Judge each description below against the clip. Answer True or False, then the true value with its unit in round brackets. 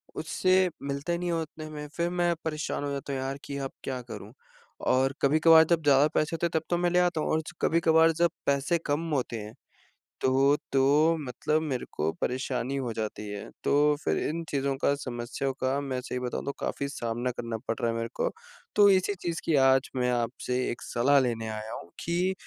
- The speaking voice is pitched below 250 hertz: True (140 Hz)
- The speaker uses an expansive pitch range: False (4.1 semitones)